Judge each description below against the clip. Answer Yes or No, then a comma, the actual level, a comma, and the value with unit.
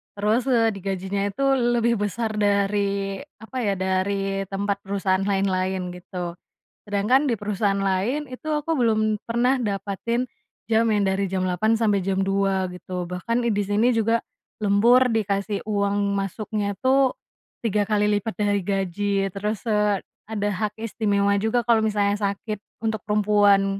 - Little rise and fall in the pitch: Yes, narrow, 2.3 semitones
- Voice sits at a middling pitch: No, high, 205 Hz